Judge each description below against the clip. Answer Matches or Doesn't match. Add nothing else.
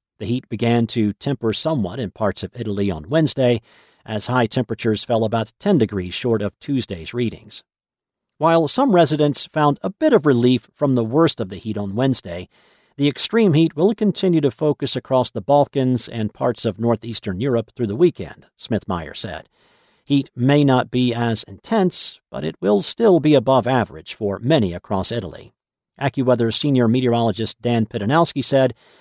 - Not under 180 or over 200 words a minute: Doesn't match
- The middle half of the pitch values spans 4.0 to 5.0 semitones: Matches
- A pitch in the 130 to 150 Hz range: Doesn't match